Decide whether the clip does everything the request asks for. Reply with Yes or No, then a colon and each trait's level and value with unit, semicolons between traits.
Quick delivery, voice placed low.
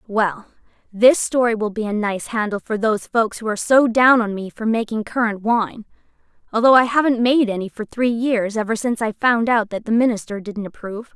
No: fast, 210 wpm; high, 225 Hz